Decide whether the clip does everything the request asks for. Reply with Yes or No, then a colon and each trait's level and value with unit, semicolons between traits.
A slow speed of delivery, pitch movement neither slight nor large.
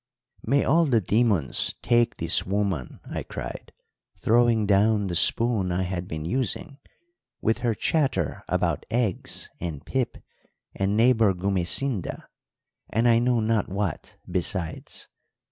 Yes: slow, 130 wpm; average, 4.5 semitones